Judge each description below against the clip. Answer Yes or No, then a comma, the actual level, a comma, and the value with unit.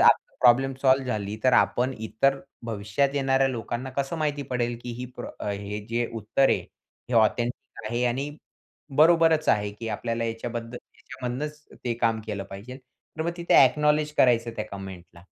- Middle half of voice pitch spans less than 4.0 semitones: Yes, average, 3.3 semitones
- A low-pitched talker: Yes, low, 120 Hz